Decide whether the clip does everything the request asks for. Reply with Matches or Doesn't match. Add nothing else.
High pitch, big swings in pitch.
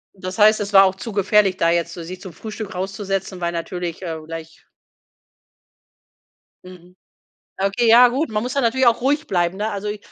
Doesn't match